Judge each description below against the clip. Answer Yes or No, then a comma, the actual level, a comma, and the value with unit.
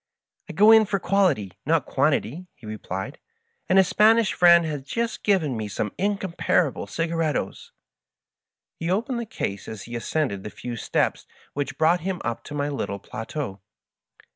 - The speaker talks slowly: No, average, 165 wpm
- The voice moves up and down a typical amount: No, wide, 8.6 semitones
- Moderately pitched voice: Yes, medium, 155 Hz